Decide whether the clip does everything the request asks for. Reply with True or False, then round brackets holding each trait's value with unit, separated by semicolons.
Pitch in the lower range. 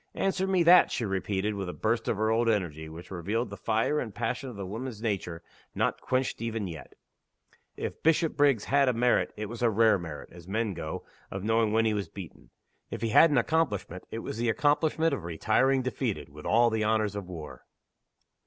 True (110 Hz)